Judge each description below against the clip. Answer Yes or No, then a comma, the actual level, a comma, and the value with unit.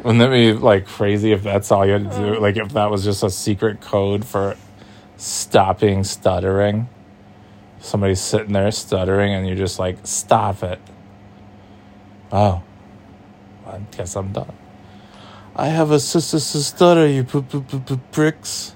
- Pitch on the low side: Yes, low, 105 Hz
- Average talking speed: Yes, average, 145 wpm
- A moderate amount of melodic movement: No, narrow, 1.8 semitones